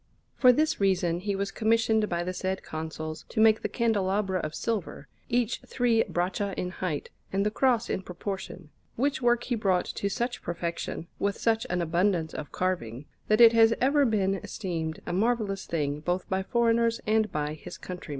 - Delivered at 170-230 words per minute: Yes, average, 180 wpm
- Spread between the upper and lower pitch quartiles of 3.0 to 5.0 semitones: Yes, average, 4.5 semitones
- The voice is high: Yes, high, 195 Hz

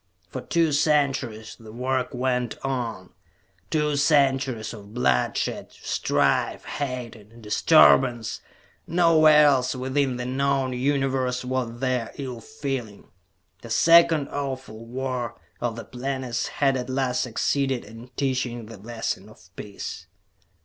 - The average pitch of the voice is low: Yes, low, 130 Hz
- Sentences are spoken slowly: Yes, slow, 125 wpm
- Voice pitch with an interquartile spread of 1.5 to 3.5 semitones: Yes, average, 2.8 semitones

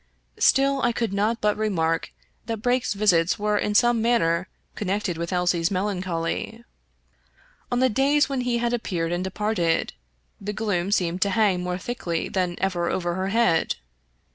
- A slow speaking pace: No, average, 160 wpm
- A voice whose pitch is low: No, high, 200 Hz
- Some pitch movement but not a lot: Yes, average, 4.4 semitones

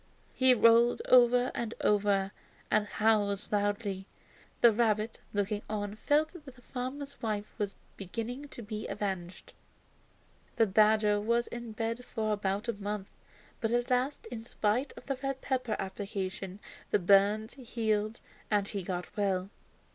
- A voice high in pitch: Yes, high, 215 Hz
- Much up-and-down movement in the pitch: No, average, 2.8 semitones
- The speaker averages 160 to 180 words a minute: No, average, 145 wpm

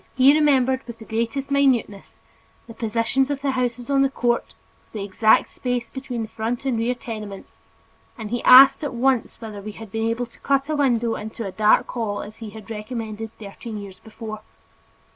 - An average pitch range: Yes, average, 3.1 semitones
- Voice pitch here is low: No, high, 230 Hz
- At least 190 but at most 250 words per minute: Yes, average, 195 wpm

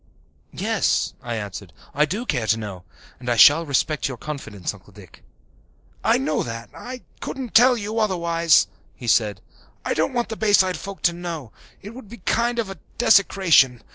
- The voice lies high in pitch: No, medium, 160 Hz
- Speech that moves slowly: No, average, 175 wpm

